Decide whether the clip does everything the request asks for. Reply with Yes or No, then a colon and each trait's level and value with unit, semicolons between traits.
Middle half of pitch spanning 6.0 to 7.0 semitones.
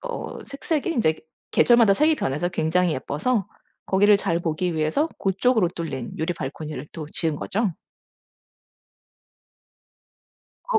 Yes: wide, 6.7 semitones